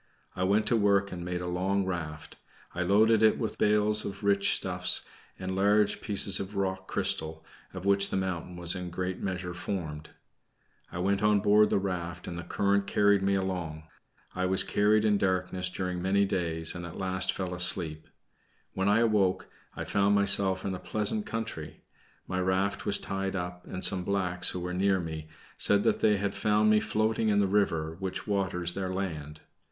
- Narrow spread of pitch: Yes, narrow, 2.1 semitones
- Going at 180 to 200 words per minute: Yes, average, 190 wpm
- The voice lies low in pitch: Yes, very low, 95 Hz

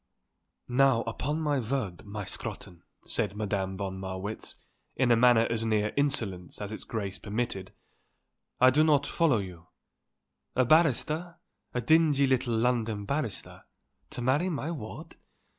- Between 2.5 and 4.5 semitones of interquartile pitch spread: No, average, 5.3 semitones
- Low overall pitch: Yes, low, 115 Hz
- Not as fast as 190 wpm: Yes, average, 140 wpm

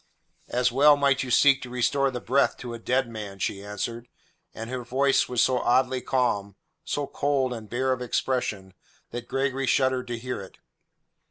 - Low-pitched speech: Yes, low, 125 Hz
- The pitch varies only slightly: Yes, narrow, 2.2 semitones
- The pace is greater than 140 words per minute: Yes, average, 180 wpm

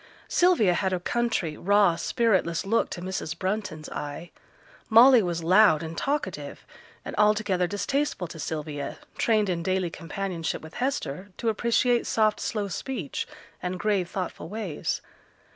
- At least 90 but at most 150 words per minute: Yes, average, 140 wpm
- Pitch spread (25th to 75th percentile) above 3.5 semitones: Yes, average, 4.5 semitones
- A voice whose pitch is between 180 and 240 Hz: Yes, high, 190 Hz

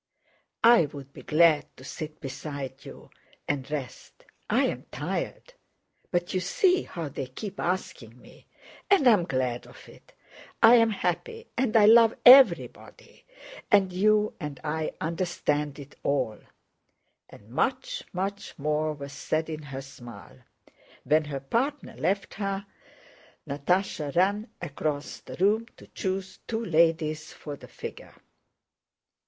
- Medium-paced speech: No, slow, 130 wpm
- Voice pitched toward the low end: No, medium, 165 Hz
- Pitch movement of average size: No, wide, 6.3 semitones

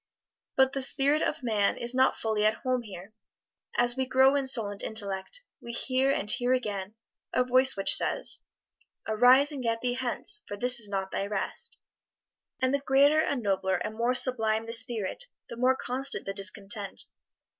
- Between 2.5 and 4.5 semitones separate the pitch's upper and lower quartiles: Yes, average, 3.9 semitones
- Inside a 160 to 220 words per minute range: Yes, average, 180 wpm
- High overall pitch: Yes, high, 240 Hz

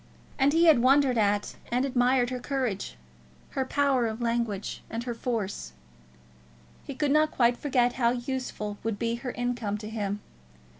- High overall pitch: Yes, high, 245 Hz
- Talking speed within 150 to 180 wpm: Yes, average, 160 wpm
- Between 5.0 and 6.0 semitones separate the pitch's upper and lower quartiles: No, average, 2.9 semitones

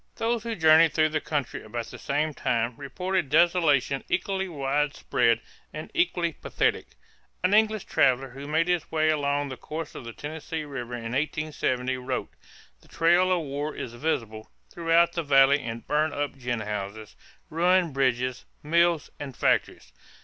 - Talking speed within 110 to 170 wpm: Yes, average, 155 wpm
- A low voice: No, medium, 150 Hz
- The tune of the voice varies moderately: Yes, average, 4.5 semitones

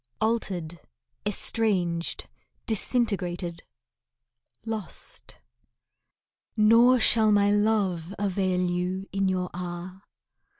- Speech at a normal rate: No, slow, 75 wpm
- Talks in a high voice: Yes, high, 195 Hz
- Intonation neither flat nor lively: Yes, average, 3.3 semitones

